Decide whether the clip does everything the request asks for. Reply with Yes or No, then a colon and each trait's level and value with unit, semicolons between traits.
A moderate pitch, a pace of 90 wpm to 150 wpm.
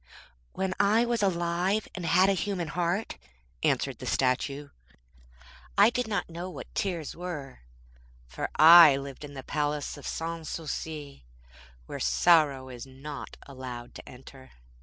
Yes: medium, 160 Hz; average, 140 wpm